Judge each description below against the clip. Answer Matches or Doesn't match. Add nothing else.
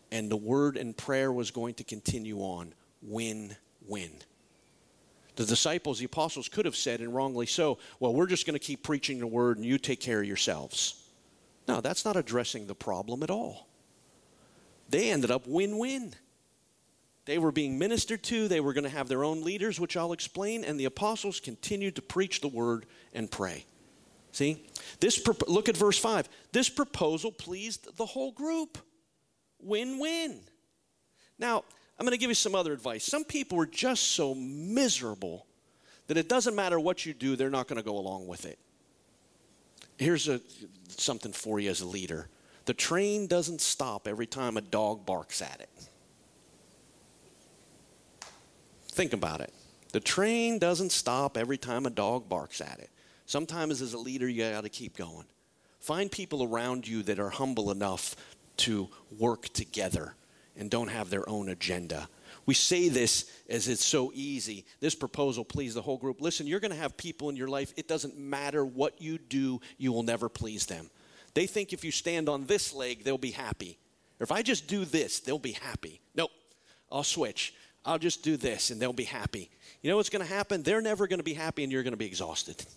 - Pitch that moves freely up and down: Matches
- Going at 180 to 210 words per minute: Matches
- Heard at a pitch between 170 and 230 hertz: Doesn't match